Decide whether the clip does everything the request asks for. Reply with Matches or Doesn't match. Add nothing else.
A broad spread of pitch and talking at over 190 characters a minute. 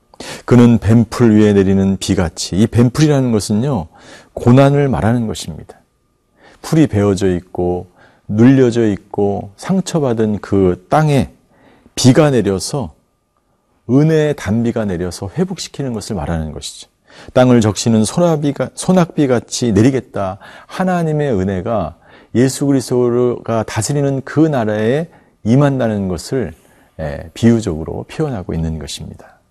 Matches